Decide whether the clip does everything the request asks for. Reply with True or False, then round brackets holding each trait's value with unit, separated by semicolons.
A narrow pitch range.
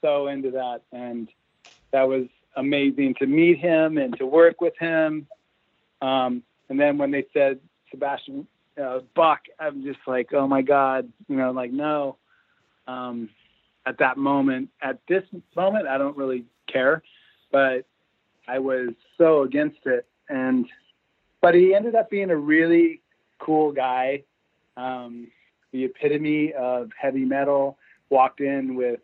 False (4.2 semitones)